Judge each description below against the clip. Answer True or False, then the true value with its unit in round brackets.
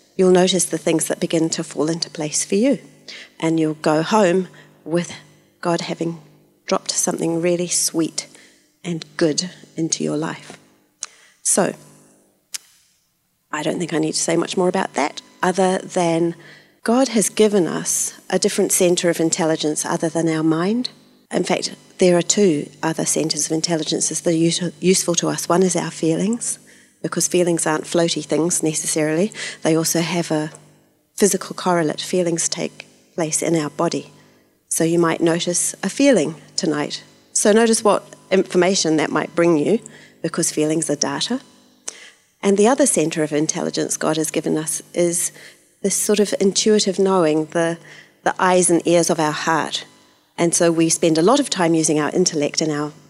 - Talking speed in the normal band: True (165 wpm)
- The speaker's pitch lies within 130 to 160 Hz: False (170 Hz)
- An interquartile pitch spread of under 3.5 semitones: True (2.5 semitones)